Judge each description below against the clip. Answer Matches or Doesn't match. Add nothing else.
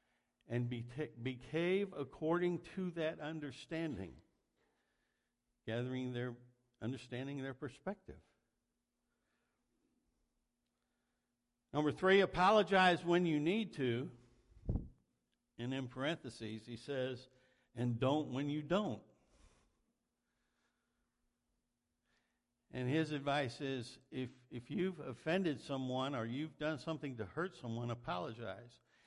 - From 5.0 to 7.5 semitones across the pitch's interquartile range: Doesn't match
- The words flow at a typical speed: Doesn't match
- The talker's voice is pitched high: Doesn't match